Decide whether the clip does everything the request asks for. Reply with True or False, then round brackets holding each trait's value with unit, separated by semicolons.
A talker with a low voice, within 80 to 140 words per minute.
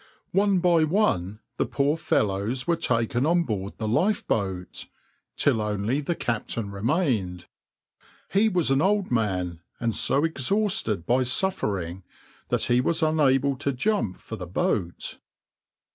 True (125 Hz; 135 wpm)